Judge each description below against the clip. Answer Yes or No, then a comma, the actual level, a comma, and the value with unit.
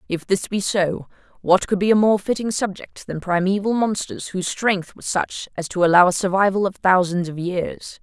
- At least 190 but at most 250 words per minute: Yes, average, 200 wpm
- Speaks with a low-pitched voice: No, high, 190 Hz